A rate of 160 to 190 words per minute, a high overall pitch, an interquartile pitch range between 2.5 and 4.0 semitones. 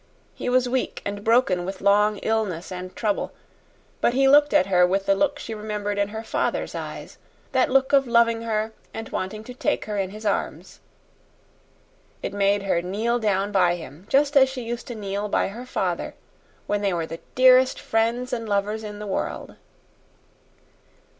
Yes: average, 180 wpm; high, 215 Hz; average, 3.6 semitones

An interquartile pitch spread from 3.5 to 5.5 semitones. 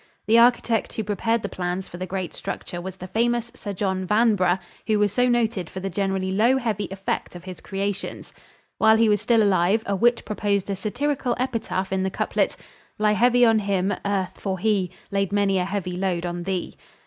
No: average, 3.0 semitones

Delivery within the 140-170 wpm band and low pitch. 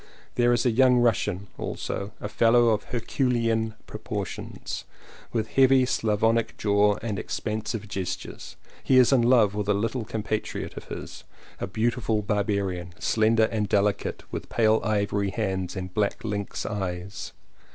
Yes: average, 150 wpm; low, 110 Hz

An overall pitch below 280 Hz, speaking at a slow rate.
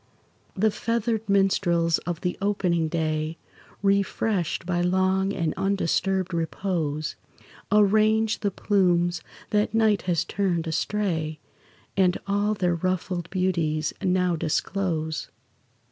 Yes: medium, 185 Hz; slow, 105 wpm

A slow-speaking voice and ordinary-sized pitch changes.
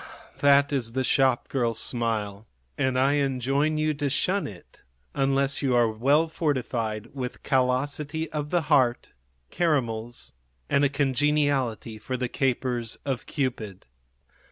Yes: slow, 130 wpm; average, 3.2 semitones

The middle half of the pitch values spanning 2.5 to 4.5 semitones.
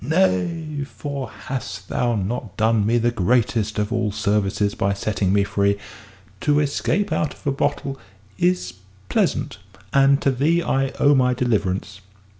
No: wide, 5.4 semitones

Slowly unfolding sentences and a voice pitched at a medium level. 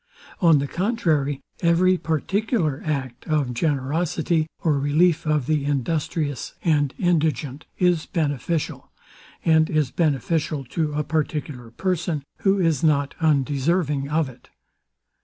Yes: slow, 120 wpm; medium, 155 Hz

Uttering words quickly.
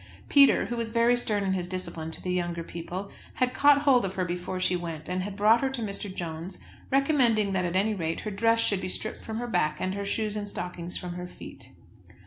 Yes: fast, 235 wpm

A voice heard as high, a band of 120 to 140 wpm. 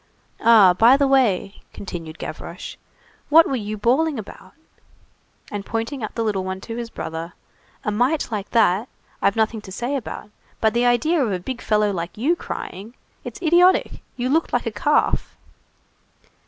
No: high, 225 Hz; average, 170 wpm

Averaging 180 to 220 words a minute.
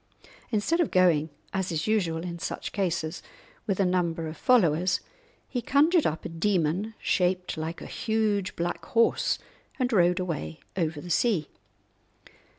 No: average, 150 wpm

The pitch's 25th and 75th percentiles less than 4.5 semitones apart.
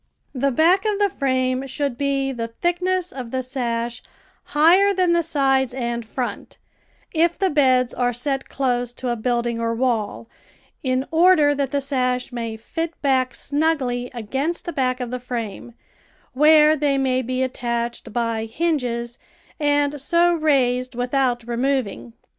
Yes: average, 3.4 semitones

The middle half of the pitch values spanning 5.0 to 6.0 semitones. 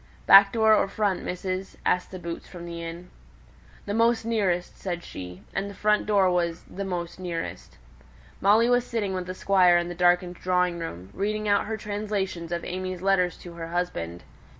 No: average, 2.7 semitones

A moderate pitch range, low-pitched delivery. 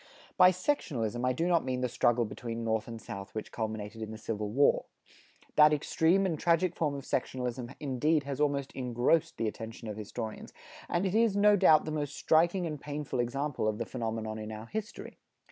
No: wide, 6.0 semitones; low, 130 Hz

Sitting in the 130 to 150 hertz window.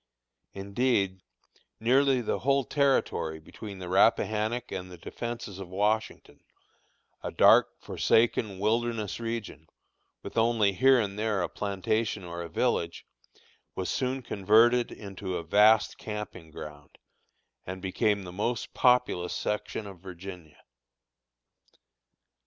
No: low, 105 Hz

